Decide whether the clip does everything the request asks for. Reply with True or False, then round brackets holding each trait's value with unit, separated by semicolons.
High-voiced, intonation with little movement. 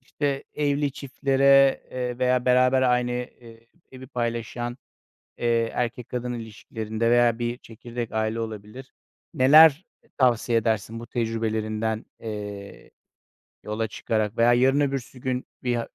False (120 Hz; 2.3 semitones)